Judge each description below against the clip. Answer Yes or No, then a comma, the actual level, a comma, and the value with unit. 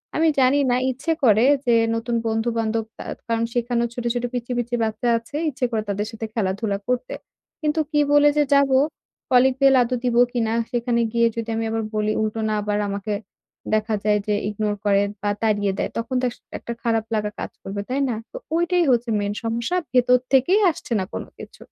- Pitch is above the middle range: Yes, high, 235 Hz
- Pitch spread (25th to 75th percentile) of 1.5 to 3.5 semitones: Yes, narrow, 2.6 semitones